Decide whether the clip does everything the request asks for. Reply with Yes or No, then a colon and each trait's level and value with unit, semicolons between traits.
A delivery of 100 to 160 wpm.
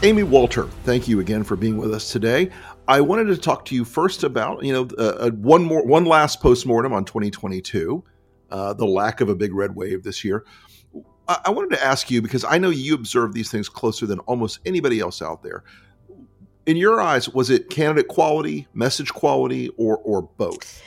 No: average, 200 wpm